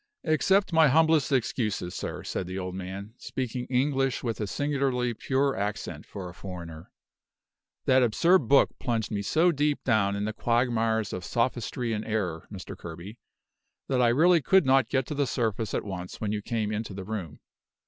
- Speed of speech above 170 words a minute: Yes, average, 180 wpm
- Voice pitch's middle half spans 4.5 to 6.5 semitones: Yes, average, 5.0 semitones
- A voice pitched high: No, low, 115 Hz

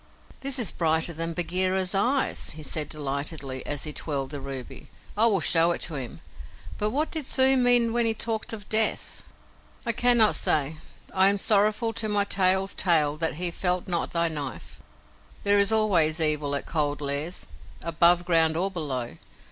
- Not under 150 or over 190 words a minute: Yes, average, 180 wpm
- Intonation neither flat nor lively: No, wide, 5.7 semitones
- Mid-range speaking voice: Yes, medium, 175 Hz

